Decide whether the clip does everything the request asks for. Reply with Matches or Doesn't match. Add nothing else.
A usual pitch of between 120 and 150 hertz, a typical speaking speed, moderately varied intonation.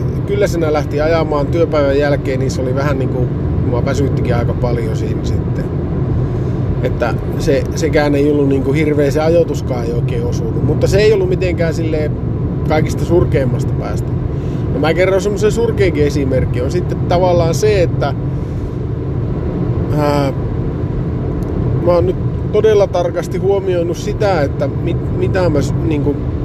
Matches